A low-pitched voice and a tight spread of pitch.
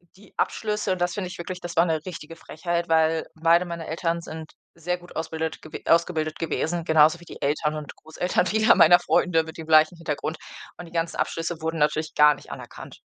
No: medium, 165 Hz; narrow, 1.7 semitones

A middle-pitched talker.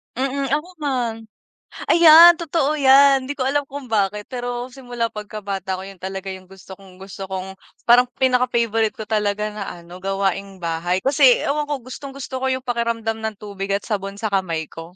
No: high, 225 Hz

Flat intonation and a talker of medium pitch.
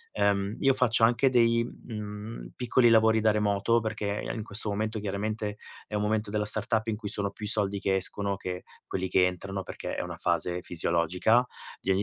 No: narrow, 2.1 semitones; low, 105 Hz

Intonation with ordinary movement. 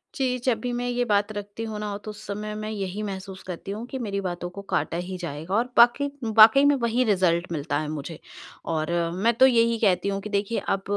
Yes: average, 3.9 semitones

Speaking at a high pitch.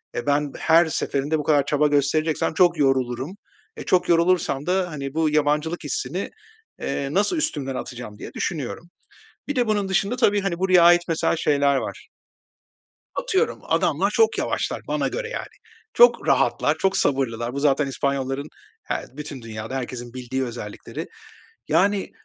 No: medium, 150 Hz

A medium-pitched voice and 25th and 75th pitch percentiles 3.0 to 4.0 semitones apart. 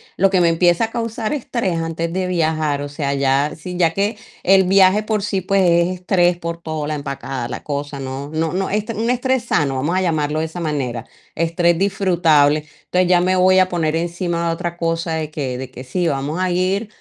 Yes: medium, 170 Hz; average, 3.6 semitones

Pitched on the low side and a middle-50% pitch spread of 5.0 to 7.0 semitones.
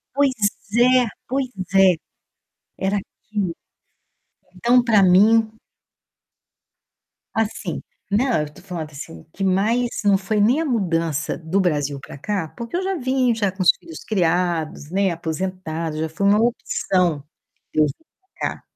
No: high, 195 Hz; wide, 5.6 semitones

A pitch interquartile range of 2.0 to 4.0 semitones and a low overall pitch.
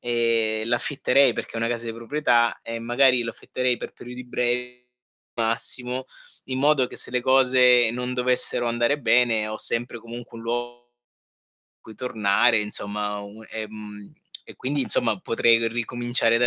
No: narrow, 1.6 semitones; low, 120 Hz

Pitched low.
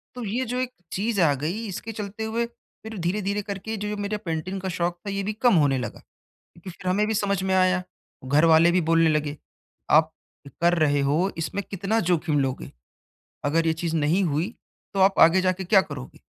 No: medium, 185 Hz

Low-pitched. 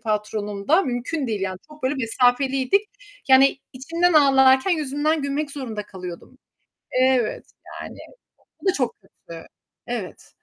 No: very high, 265 Hz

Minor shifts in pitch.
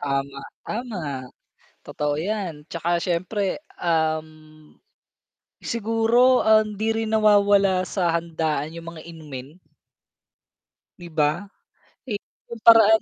No: wide, 5.4 semitones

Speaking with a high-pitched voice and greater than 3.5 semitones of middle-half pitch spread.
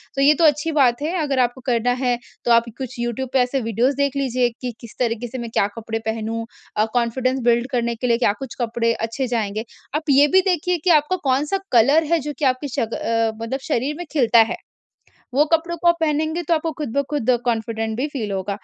Yes: very high, 255 Hz; average, 4.1 semitones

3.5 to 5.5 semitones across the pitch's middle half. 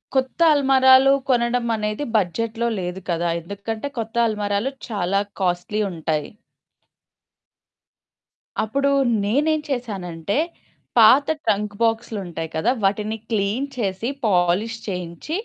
Yes: average, 4.2 semitones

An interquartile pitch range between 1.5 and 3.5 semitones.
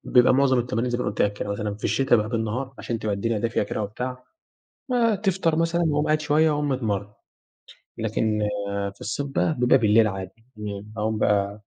No: average, 4.9 semitones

